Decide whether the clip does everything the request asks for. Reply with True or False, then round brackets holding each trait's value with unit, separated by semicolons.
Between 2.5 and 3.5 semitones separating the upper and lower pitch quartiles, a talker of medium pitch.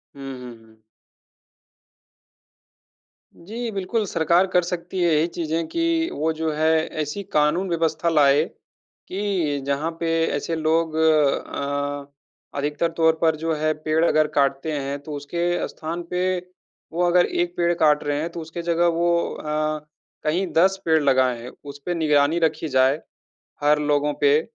True (2.9 semitones; 160 Hz)